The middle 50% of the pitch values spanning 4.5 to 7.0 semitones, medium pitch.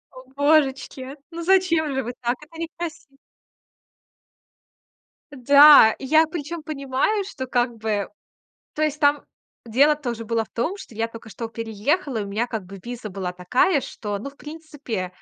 No: average, 5.1 semitones; very high, 265 Hz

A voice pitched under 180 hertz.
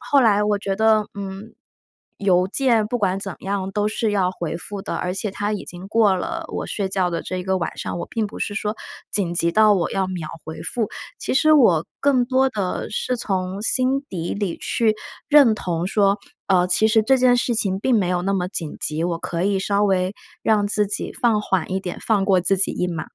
No: high, 200 Hz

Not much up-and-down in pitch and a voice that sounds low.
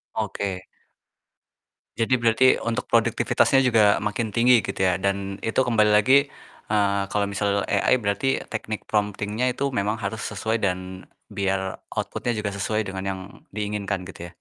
Yes: narrow, 2.1 semitones; low, 105 Hz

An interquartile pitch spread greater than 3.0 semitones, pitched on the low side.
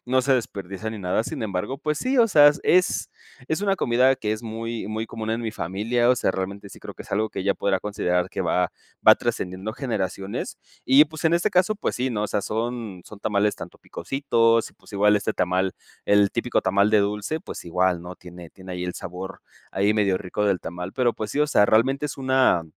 Yes: average, 4.7 semitones; low, 105 Hz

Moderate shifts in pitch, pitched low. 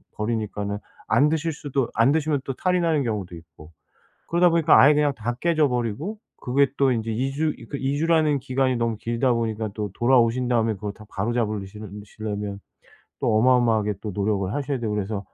Yes: average, 4.9 semitones; low, 120 Hz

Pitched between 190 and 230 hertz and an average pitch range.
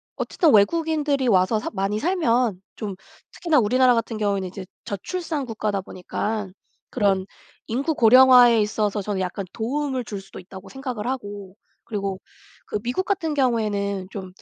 Yes: high, 220 Hz; average, 4.7 semitones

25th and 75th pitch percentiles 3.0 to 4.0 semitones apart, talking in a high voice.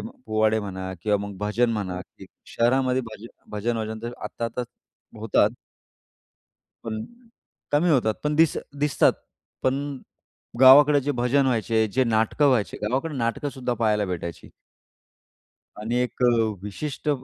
No: average, 3.6 semitones; low, 120 Hz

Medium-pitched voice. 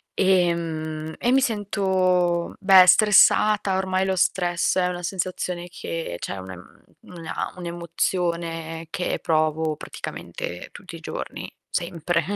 Yes: medium, 175 Hz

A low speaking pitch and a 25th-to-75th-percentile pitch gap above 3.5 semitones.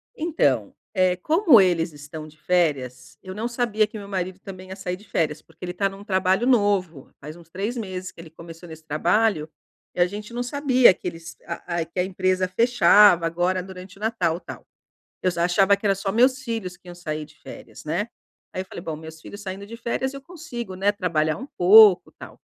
No: medium, 185 Hz; average, 3.9 semitones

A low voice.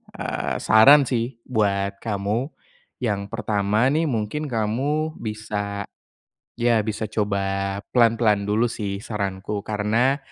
Yes: low, 110 Hz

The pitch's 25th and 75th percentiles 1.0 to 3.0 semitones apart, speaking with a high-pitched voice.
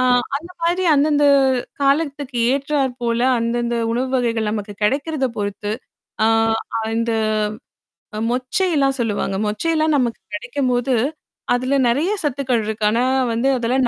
No: average, 3.6 semitones; very high, 255 Hz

